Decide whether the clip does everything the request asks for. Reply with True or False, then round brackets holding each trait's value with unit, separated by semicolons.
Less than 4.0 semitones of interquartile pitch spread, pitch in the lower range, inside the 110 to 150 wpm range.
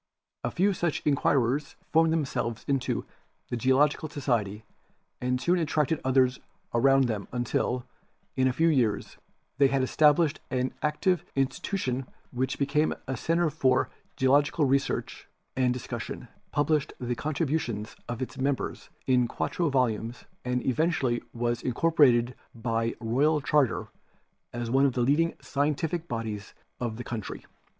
True (3.6 semitones; 130 Hz; 140 wpm)